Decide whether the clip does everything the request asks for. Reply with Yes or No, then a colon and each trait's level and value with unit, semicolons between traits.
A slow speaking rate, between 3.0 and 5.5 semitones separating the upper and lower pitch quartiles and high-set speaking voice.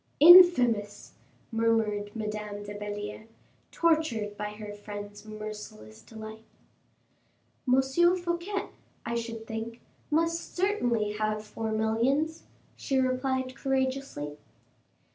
Yes: slow, 95 wpm; average, 4.2 semitones; high, 225 Hz